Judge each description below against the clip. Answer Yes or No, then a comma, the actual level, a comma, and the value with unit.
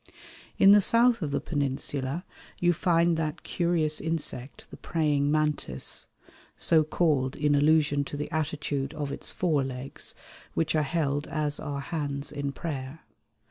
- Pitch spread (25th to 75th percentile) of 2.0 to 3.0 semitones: Yes, narrow, 2.4 semitones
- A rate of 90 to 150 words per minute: Yes, average, 140 wpm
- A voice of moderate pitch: Yes, medium, 150 Hz